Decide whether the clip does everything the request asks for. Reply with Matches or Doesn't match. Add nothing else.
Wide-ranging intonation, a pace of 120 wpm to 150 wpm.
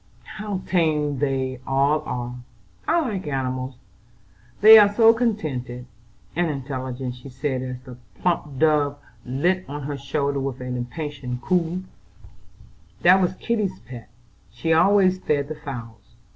Matches